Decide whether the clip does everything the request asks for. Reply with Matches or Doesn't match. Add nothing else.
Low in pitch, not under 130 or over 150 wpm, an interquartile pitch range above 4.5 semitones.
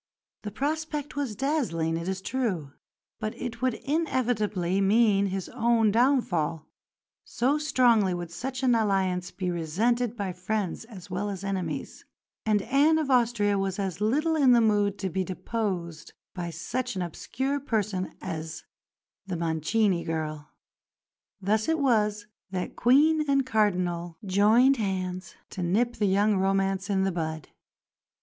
Doesn't match